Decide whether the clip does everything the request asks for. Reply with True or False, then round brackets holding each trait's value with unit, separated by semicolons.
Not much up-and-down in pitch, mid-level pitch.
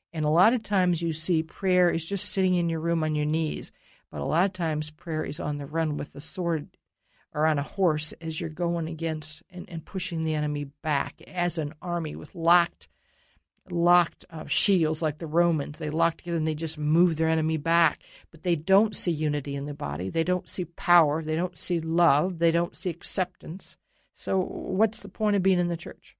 True (2.2 semitones; 165 Hz)